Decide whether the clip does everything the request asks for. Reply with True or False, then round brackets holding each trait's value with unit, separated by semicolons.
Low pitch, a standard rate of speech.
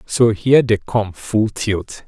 True (110 Hz; 175 wpm)